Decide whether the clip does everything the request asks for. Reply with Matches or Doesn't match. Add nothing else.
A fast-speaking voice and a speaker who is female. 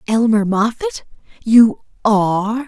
Doesn't match